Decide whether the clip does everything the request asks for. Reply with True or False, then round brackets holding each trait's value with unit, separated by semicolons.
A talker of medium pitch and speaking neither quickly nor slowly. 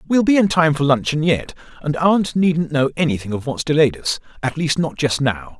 False (150 Hz; 215 wpm)